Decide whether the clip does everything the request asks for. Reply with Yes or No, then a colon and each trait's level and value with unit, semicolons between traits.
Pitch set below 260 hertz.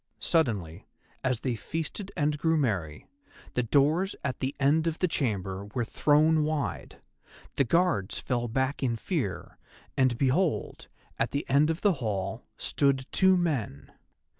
Yes: low, 135 Hz